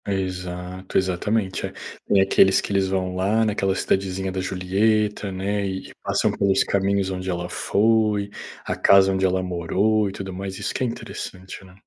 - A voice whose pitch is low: Yes, very low, 95 Hz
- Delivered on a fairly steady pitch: Yes, narrow, 1.4 semitones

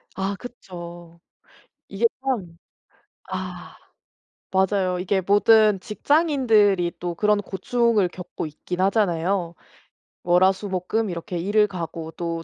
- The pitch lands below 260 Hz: Yes, high, 190 Hz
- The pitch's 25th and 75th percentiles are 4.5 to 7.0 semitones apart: No, average, 3.3 semitones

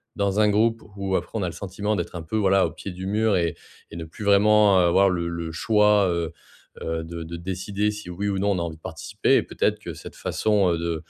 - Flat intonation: No, average, 3.3 semitones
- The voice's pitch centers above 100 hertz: No, very low, 95 Hz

